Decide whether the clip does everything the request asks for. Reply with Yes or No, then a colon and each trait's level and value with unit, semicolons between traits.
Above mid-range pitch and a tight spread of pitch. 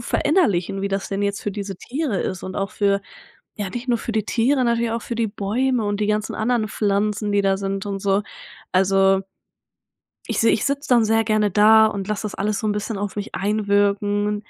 Yes: high, 210 Hz; narrow, 2.0 semitones